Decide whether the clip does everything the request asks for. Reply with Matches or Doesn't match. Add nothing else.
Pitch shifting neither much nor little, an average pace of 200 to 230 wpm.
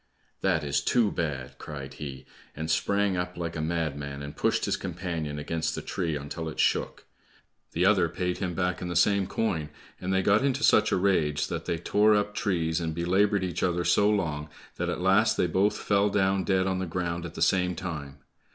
Matches